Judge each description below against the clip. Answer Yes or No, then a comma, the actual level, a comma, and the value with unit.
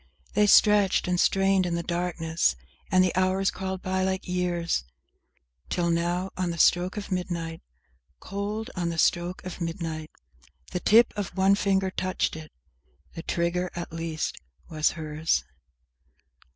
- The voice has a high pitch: No, medium, 180 Hz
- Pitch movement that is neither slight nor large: No, narrow, 2.0 semitones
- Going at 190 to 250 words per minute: No, average, 145 wpm